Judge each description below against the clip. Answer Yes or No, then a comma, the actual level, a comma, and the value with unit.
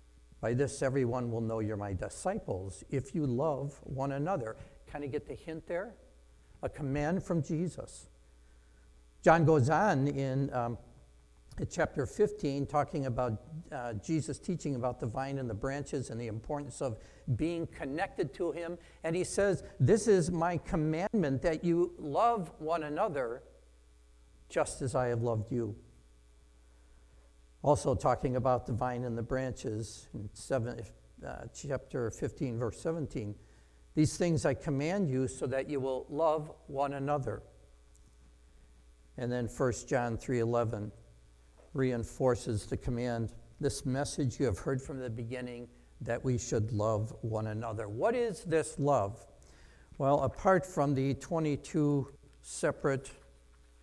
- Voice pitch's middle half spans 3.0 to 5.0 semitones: No, wide, 5.6 semitones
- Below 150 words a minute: Yes, average, 140 wpm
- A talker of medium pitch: No, low, 130 Hz